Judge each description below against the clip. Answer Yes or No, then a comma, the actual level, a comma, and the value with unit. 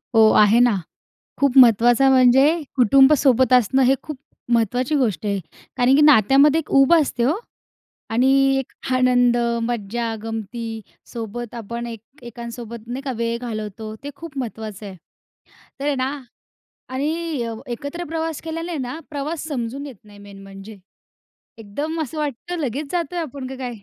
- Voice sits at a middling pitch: No, very high, 250 Hz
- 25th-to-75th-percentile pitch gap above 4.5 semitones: No, average, 3.8 semitones